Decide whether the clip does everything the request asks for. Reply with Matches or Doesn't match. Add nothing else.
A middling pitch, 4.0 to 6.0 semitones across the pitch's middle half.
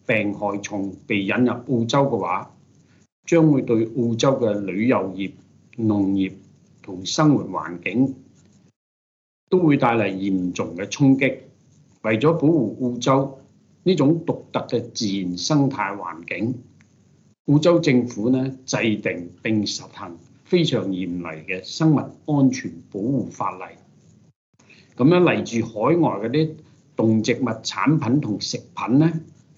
Doesn't match